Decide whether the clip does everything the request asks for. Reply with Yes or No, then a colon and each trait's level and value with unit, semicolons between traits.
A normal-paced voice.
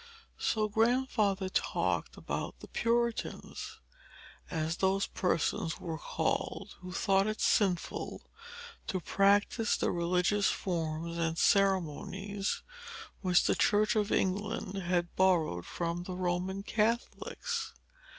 No: slow, 110 wpm